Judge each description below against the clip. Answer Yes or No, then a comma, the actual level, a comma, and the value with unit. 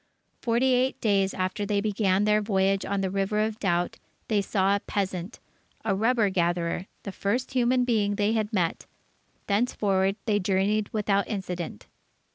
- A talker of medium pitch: No, high, 200 Hz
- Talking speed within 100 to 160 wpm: Yes, average, 155 wpm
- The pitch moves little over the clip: Yes, narrow, 2.1 semitones